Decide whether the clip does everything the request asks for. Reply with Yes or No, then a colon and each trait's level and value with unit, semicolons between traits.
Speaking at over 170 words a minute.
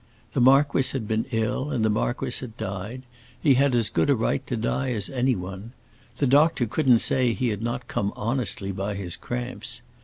Yes: average, 190 wpm